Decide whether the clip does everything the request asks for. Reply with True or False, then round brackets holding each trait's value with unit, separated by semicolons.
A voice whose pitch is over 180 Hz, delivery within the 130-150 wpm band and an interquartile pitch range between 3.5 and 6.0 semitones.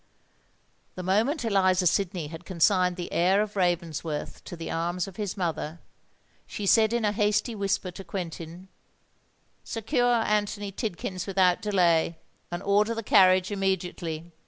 False (190 Hz; 140 wpm; 3.0 semitones)